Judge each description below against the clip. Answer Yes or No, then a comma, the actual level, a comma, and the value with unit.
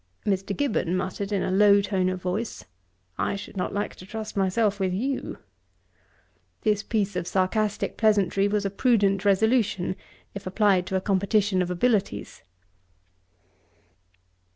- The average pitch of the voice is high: Yes, high, 200 Hz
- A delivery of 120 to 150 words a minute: Yes, average, 140 wpm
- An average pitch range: No, narrow, 2.1 semitones